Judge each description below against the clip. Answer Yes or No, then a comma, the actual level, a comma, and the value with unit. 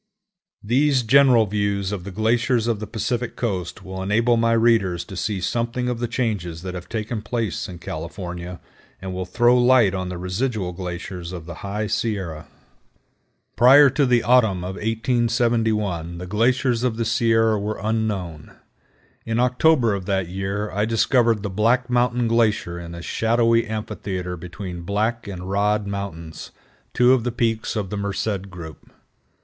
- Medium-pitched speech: No, low, 105 Hz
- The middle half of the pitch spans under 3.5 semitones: No, average, 4.1 semitones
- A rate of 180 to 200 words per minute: No, average, 160 wpm